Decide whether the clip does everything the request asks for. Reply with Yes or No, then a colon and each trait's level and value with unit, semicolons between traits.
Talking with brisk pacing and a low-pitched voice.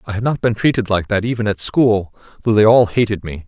Yes: fast, 260 wpm; low, 105 Hz